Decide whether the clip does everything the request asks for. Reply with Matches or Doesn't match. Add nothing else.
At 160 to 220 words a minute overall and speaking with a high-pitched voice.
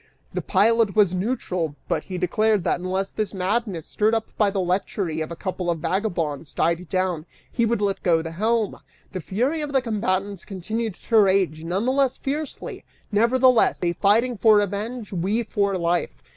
Matches